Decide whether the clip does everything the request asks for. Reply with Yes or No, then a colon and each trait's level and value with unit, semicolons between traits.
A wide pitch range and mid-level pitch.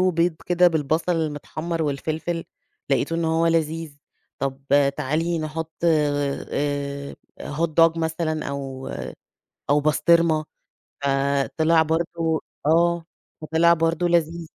No: narrow, 2.4 semitones; medium, 160 Hz